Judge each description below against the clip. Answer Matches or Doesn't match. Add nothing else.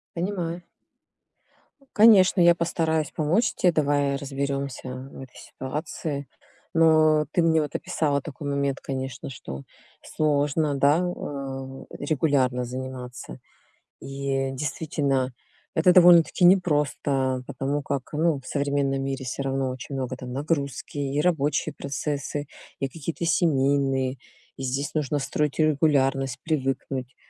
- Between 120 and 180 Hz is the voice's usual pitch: Matches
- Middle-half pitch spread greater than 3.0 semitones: Doesn't match